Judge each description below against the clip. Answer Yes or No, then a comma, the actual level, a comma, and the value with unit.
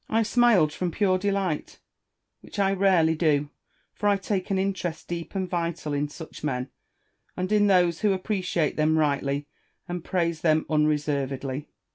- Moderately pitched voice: Yes, medium, 170 Hz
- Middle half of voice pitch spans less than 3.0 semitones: No, average, 4.2 semitones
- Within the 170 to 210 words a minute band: No, average, 160 wpm